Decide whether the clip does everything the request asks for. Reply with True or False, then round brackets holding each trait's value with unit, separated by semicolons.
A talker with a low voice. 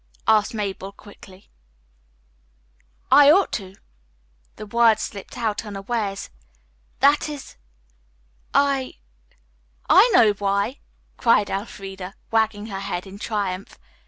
False (205 Hz)